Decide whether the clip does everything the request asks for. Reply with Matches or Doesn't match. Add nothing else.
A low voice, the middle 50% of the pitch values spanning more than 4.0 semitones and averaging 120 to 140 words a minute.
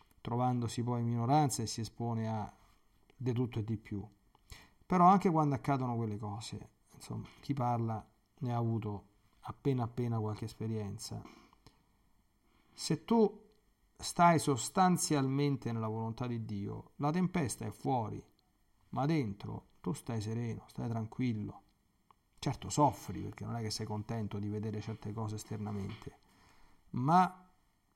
Matches